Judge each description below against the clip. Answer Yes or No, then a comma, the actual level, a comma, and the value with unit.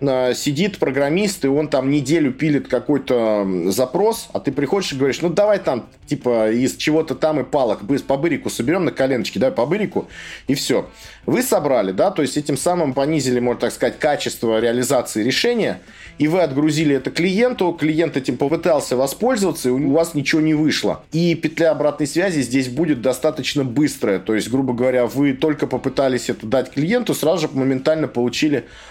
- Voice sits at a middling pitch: Yes, medium, 145 Hz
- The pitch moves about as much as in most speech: Yes, average, 3.7 semitones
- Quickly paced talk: Yes, fast, 170 wpm